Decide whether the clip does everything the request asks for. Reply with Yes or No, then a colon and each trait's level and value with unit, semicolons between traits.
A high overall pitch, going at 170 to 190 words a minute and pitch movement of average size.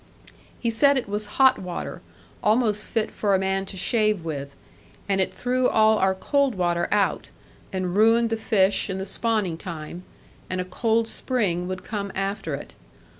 Yes: high, 200 Hz; average, 175 wpm; average, 3.3 semitones